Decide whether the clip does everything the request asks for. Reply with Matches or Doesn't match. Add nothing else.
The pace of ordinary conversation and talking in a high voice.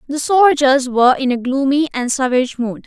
Matches